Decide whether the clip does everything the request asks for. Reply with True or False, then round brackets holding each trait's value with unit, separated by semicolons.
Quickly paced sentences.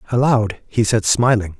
False (150 wpm)